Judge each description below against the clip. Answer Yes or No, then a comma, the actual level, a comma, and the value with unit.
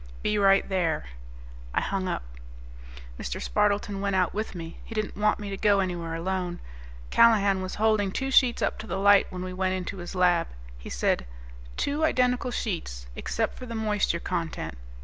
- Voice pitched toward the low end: No, high, 195 Hz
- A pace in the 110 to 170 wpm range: No, average, 180 wpm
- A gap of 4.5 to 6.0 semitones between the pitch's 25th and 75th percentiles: No, average, 2.9 semitones